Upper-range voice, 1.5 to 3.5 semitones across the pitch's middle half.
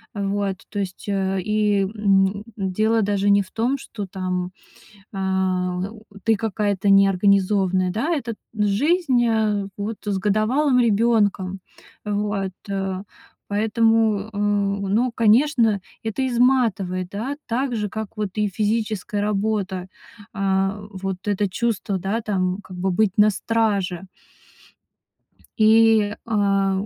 Yes: high, 205 Hz; narrow, 2.4 semitones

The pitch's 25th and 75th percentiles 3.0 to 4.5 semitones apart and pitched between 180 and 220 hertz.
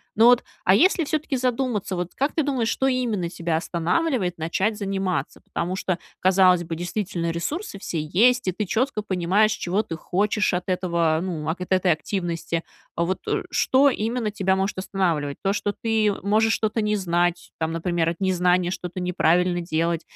Yes: average, 3.8 semitones; medium, 185 Hz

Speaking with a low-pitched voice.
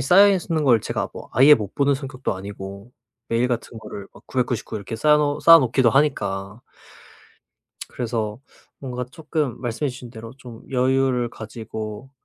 Yes: low, 125 Hz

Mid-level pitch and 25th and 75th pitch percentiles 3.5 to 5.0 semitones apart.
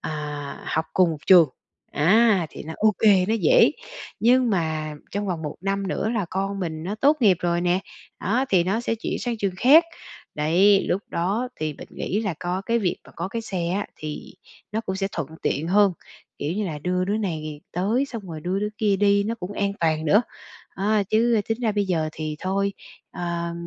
No: high, 195 Hz; average, 3.9 semitones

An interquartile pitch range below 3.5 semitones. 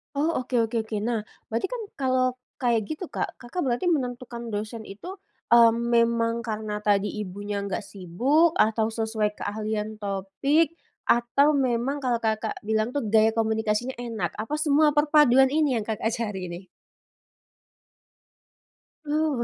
No: average, 3.8 semitones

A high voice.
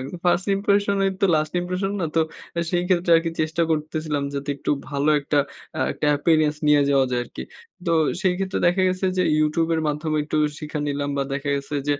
No: medium, 155 Hz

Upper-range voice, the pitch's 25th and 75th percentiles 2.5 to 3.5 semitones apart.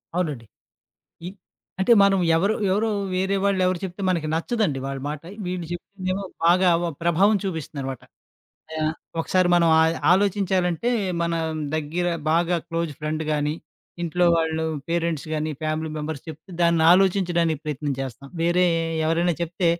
No: medium, 170 Hz; average, 2.8 semitones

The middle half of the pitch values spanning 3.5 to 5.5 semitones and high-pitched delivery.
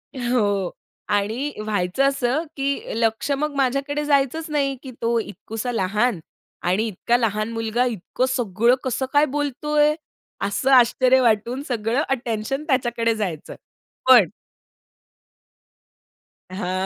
Yes: average, 4.2 semitones; high, 240 Hz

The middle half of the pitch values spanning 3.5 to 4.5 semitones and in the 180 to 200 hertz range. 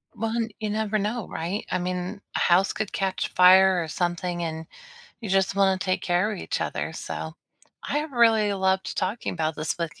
No: average, 3.0 semitones; high, 190 Hz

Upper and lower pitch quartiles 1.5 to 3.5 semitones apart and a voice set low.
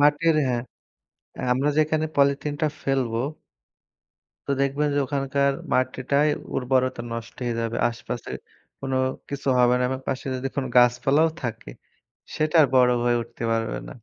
Yes: average, 2.8 semitones; low, 130 Hz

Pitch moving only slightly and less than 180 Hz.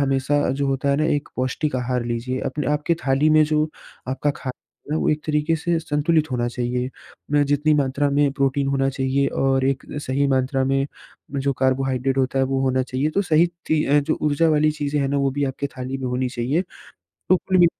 Yes: narrow, 2.1 semitones; medium, 140 Hz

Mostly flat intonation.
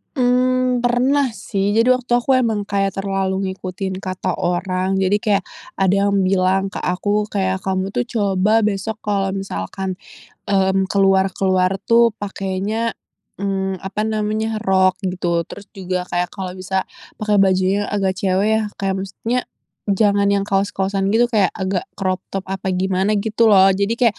Yes: narrow, 2.0 semitones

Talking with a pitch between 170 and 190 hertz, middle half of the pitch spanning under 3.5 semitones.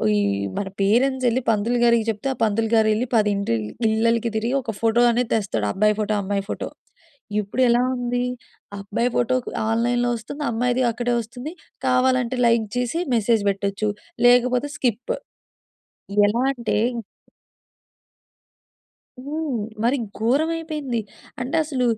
No: high, 235 Hz; narrow, 2.6 semitones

